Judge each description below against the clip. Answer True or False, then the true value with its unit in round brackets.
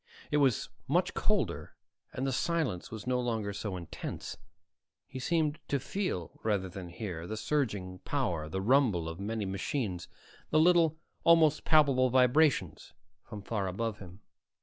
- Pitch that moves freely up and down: True (7.1 semitones)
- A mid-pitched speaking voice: False (115 Hz)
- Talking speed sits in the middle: True (150 wpm)